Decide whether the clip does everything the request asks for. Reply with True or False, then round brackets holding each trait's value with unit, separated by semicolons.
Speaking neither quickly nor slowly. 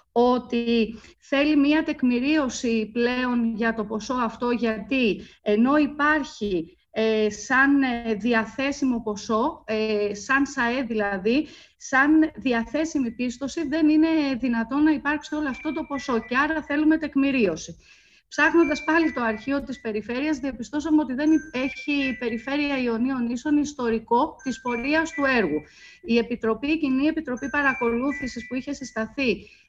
True (130 wpm)